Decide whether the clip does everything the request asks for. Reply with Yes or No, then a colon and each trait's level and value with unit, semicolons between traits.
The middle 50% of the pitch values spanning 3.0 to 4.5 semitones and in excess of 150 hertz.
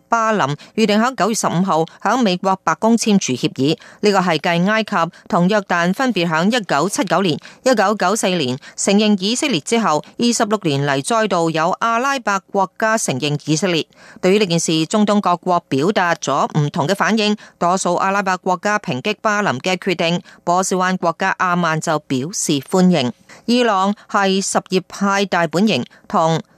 Yes: average, 4.2 semitones; high, 190 Hz